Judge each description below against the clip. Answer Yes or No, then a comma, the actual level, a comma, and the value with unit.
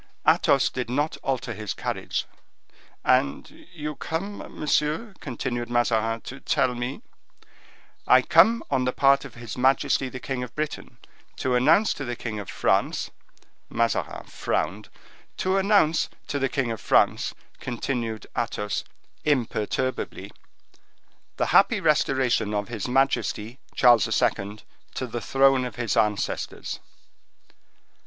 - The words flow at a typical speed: No, slow, 125 wpm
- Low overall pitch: Yes, low, 130 Hz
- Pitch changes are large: No, average, 3.4 semitones